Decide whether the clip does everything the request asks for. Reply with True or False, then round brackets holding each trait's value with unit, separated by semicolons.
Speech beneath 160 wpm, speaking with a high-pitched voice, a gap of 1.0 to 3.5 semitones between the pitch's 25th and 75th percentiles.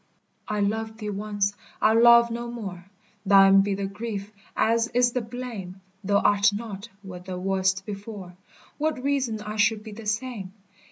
False (165 wpm; 210 Hz; 2.9 semitones)